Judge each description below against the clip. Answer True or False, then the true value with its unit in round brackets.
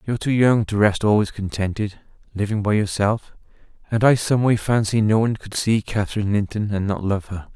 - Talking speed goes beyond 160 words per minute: True (200 wpm)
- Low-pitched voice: True (105 Hz)